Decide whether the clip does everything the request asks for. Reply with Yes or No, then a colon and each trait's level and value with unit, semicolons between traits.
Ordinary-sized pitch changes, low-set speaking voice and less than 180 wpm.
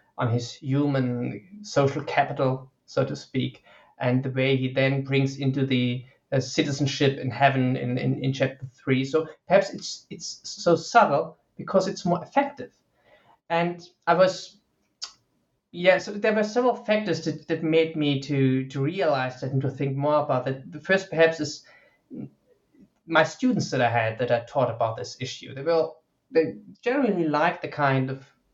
No: average, 4.3 semitones; medium, 145 Hz; average, 170 wpm